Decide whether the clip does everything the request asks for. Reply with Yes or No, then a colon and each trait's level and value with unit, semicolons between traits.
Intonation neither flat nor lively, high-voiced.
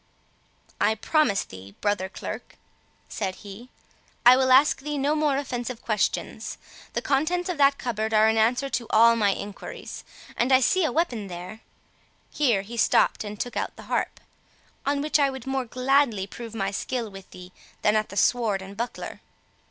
Yes: average, 4.7 semitones; high, 235 Hz